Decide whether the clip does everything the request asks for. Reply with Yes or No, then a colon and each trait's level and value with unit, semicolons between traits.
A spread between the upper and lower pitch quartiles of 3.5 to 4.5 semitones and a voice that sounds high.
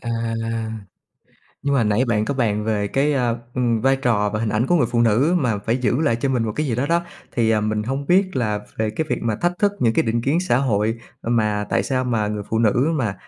No: average, 3.9 semitones; low, 120 Hz